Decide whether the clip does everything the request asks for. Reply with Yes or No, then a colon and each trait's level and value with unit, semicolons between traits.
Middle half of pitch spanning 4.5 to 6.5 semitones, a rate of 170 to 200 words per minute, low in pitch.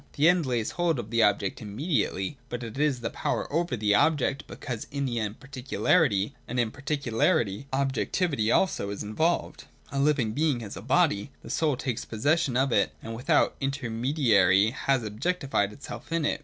Yes: average, 5.0 semitones; average, 180 wpm; low, 130 Hz